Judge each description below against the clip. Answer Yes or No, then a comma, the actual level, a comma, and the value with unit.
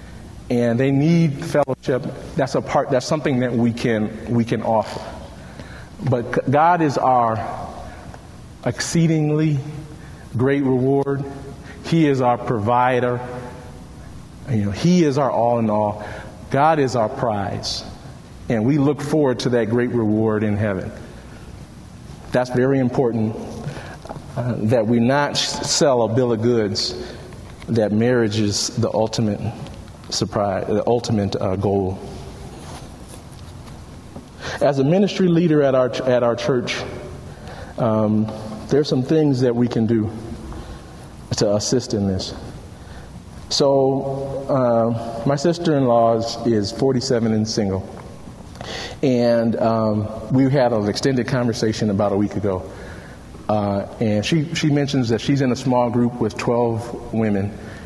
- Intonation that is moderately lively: Yes, average, 3.8 semitones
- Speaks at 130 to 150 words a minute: Yes, slow, 135 wpm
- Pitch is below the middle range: Yes, low, 120 Hz